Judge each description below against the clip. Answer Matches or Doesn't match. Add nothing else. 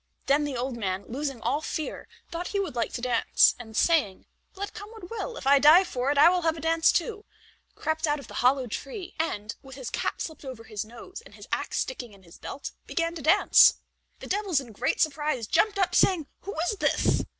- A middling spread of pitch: Doesn't match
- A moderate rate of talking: Doesn't match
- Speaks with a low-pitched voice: Doesn't match